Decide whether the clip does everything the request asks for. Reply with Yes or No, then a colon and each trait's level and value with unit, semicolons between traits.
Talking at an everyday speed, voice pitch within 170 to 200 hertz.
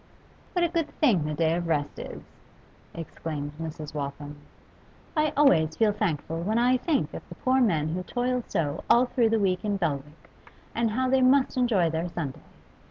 Yes: average, 180 wpm; medium, 185 Hz